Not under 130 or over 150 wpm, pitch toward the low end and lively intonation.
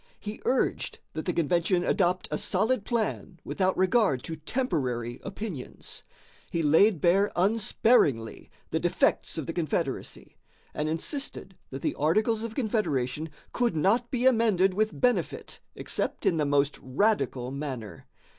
No: slow, 135 wpm; medium, 185 Hz; wide, 6.7 semitones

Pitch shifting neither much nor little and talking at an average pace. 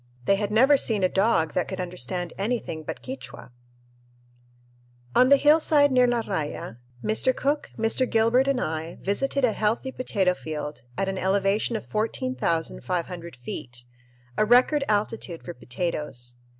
No: wide, 6.7 semitones; average, 145 wpm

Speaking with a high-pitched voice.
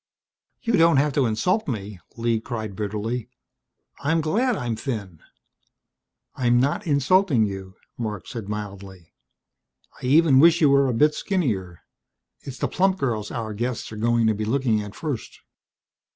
No: low, 120 Hz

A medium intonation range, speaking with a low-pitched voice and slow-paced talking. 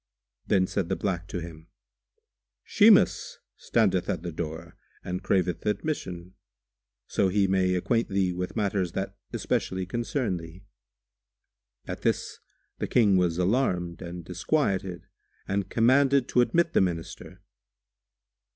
Yes: average, 3.0 semitones; very low, 95 Hz; slow, 125 wpm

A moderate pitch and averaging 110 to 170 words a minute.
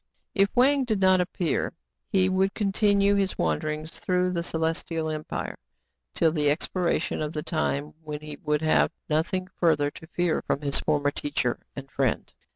Yes: medium, 160 Hz; average, 160 wpm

